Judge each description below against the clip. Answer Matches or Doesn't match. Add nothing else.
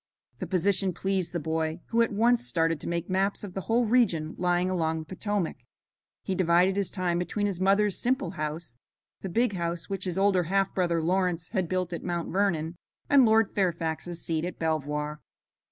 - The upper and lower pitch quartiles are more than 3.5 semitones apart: Doesn't match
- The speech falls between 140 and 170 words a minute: Doesn't match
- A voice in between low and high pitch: Matches